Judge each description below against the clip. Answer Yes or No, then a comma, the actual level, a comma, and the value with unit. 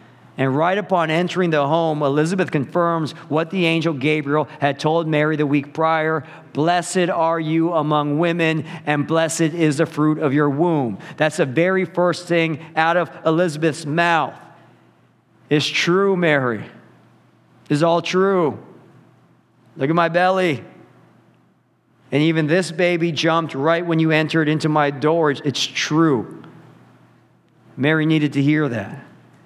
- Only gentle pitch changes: Yes, narrow, 2.0 semitones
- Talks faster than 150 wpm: No, average, 140 wpm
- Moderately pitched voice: Yes, medium, 160 Hz